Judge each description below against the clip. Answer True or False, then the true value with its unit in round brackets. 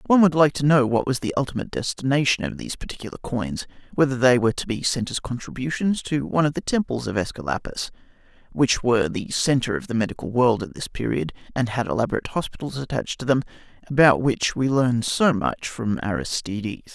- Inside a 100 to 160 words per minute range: False (190 wpm)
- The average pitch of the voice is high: False (130 Hz)